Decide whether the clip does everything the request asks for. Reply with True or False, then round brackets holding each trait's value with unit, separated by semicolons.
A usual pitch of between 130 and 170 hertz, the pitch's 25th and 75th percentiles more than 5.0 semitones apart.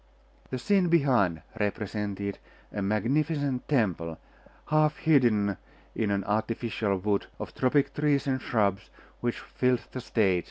False (115 Hz; 5.4 semitones)